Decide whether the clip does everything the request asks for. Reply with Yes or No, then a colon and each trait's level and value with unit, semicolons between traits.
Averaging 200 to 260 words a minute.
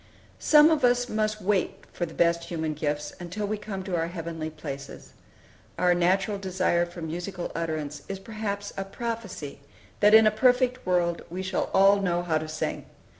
No: average, 175 wpm